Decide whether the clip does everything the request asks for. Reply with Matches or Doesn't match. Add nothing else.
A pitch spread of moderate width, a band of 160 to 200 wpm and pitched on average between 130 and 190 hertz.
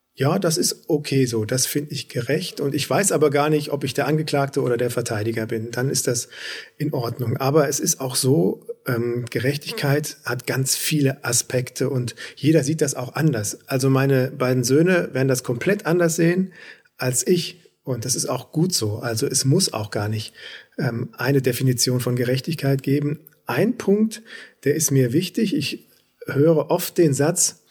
Matches